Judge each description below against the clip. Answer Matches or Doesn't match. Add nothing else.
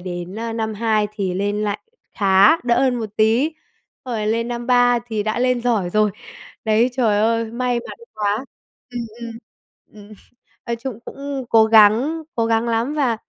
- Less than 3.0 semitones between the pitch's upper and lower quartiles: Matches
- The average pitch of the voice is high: Matches